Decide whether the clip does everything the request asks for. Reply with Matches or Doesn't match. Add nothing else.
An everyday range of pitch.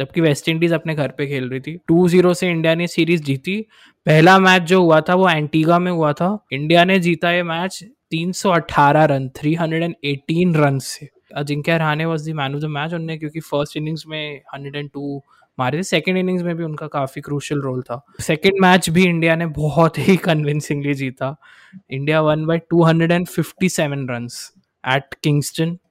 Matches